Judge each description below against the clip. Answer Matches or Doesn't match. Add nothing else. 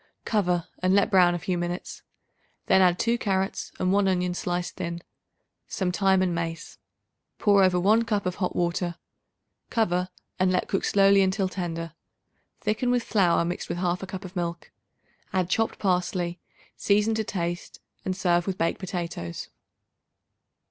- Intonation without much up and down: Matches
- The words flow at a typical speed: Matches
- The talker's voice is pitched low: Doesn't match